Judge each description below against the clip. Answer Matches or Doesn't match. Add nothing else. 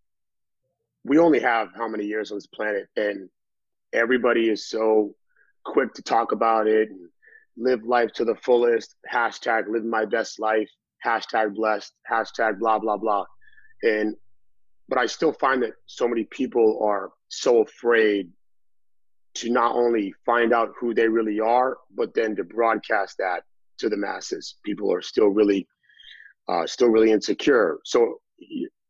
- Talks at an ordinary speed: Matches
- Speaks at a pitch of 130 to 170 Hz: Doesn't match